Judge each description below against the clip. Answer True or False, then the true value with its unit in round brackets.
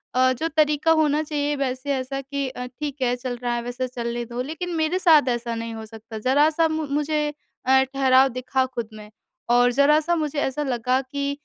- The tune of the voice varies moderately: True (3.3 semitones)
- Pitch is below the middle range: False (265 Hz)